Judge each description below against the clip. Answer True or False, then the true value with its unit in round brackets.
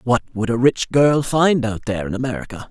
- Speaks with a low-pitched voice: True (120 Hz)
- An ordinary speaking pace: False (220 wpm)